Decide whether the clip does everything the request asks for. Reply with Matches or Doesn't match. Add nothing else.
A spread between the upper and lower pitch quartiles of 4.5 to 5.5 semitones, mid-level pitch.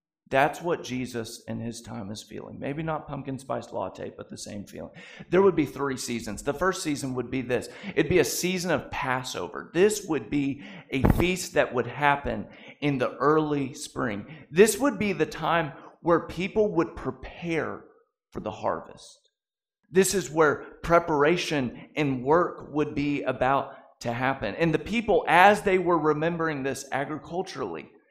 Matches